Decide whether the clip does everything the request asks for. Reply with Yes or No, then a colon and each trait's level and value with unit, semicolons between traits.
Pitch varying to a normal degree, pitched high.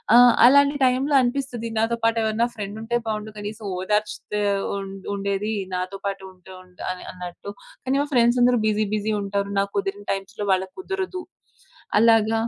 Yes: average, 3.5 semitones; high, 215 Hz